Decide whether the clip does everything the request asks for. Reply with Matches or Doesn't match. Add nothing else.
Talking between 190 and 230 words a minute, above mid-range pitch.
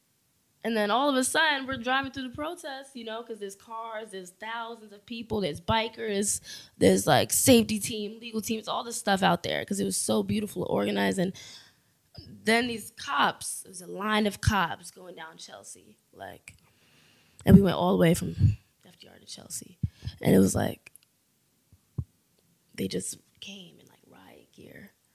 Doesn't match